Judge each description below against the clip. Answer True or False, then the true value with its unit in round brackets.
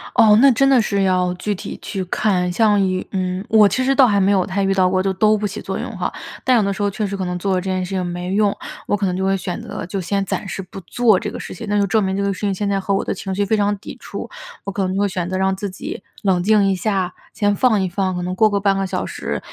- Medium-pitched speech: False (195 Hz)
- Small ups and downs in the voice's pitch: True (1.8 semitones)